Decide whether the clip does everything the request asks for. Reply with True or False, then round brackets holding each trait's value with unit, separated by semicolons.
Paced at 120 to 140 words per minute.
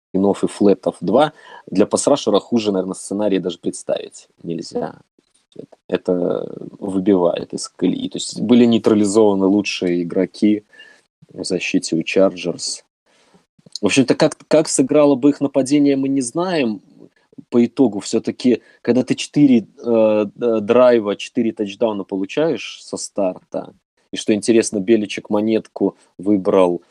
True (125 wpm)